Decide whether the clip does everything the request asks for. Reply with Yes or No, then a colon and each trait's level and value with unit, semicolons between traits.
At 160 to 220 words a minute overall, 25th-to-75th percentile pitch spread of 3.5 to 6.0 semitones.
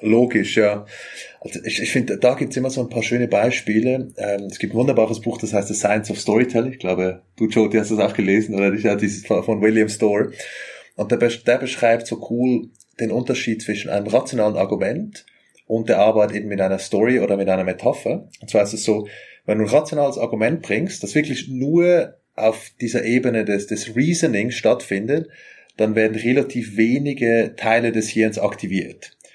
No: average, 185 wpm; narrow, 2.6 semitones